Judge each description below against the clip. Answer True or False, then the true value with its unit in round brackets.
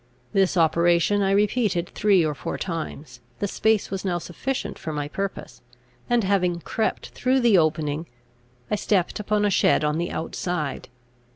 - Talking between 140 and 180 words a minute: True (160 wpm)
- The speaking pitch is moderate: True (180 Hz)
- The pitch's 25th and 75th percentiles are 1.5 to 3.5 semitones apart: False (4.1 semitones)